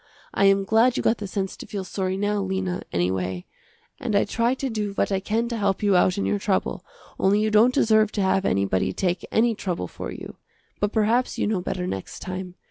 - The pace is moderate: No, fast, 220 wpm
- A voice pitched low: No, high, 200 Hz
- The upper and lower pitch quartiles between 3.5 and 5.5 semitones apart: No, average, 2.8 semitones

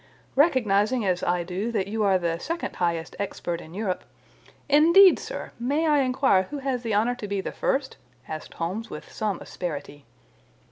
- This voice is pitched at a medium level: No, high, 210 Hz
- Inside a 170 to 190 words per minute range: Yes, average, 175 wpm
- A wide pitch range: Yes, wide, 6.6 semitones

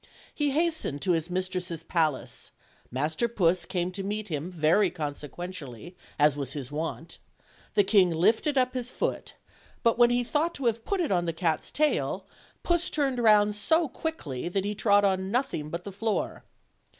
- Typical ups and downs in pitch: No, wide, 6.5 semitones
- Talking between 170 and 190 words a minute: Yes, average, 175 wpm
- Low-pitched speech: No, high, 190 Hz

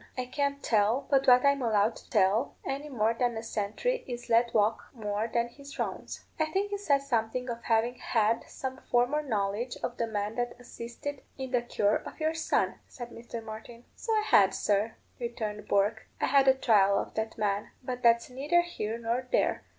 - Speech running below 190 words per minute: No, average, 195 wpm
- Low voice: No, high, 235 Hz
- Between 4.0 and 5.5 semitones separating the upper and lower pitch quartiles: No, average, 3.3 semitones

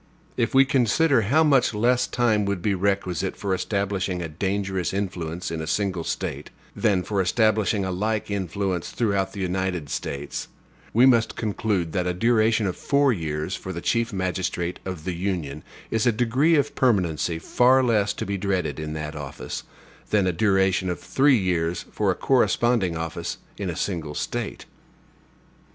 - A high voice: No, very low, 95 Hz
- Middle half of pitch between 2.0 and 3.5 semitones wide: No, average, 3.9 semitones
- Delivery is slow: No, average, 170 wpm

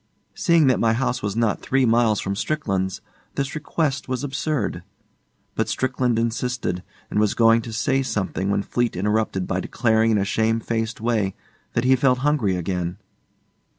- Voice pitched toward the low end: Yes, low, 115 Hz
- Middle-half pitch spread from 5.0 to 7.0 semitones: No, average, 4.1 semitones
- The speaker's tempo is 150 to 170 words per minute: Yes, average, 160 wpm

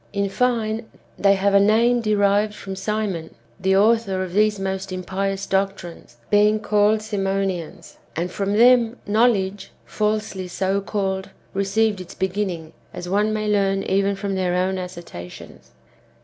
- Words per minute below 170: Yes, average, 150 wpm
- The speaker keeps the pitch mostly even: Yes, narrow, 1.9 semitones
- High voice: Yes, high, 195 Hz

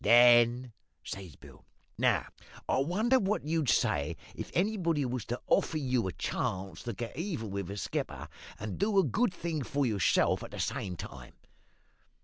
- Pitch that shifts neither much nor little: No, wide, 8.4 semitones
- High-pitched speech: No, low, 125 Hz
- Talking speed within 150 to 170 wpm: Yes, average, 165 wpm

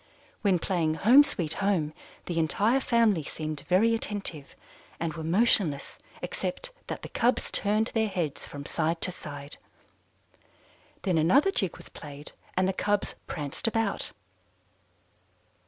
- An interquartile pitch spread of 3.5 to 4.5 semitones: No, wide, 5.6 semitones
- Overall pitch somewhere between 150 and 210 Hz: Yes, medium, 185 Hz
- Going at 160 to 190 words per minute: No, slow, 135 wpm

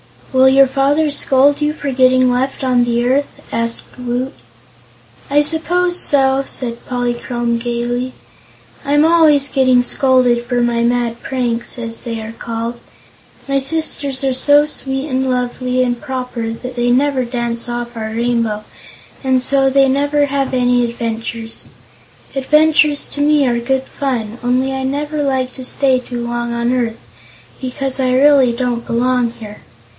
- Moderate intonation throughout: No, narrow, 2.3 semitones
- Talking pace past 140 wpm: Yes, average, 150 wpm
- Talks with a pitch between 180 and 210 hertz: No, very high, 255 Hz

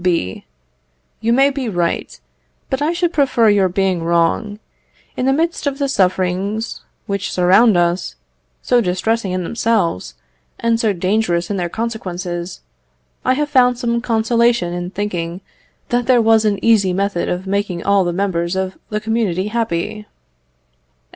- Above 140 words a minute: Yes, average, 150 wpm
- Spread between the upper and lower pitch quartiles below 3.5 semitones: No, average, 4.5 semitones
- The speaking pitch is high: Yes, high, 205 Hz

